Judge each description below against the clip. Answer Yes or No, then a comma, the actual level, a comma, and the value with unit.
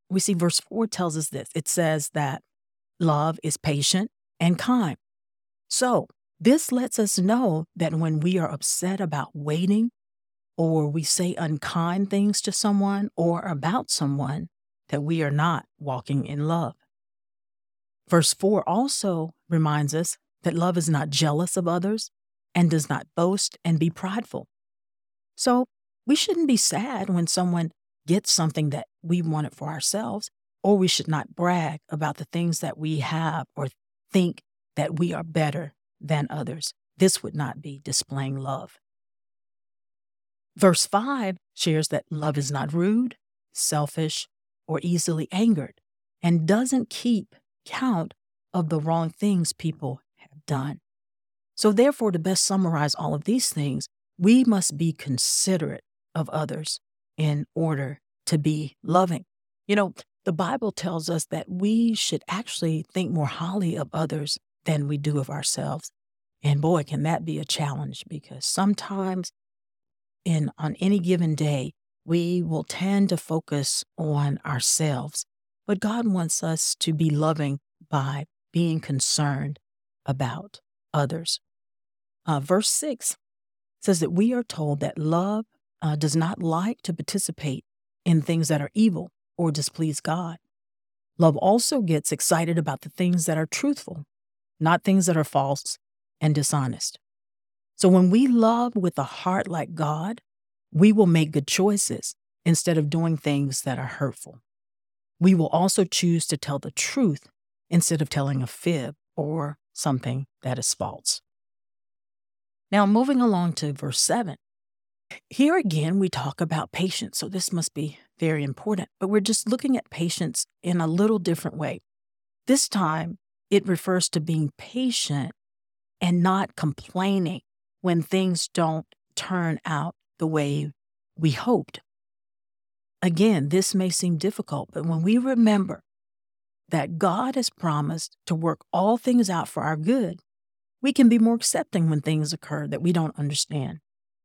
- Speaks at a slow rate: No, average, 150 wpm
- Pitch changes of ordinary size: Yes, average, 4.5 semitones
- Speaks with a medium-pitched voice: Yes, medium, 160 Hz